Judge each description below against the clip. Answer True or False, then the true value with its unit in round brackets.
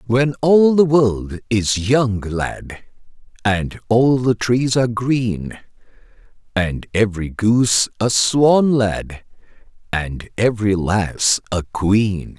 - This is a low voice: True (110 Hz)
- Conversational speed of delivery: False (115 wpm)